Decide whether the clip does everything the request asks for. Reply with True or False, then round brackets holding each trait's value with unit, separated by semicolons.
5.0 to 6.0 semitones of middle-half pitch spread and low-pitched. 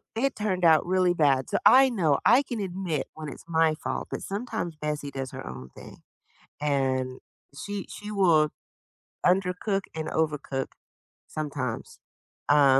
False (5.3 semitones; 160 Hz)